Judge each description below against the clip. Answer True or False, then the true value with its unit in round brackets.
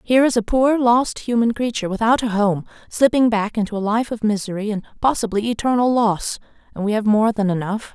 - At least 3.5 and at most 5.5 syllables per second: False (5.8 syllables/s)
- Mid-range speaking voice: False (220 Hz)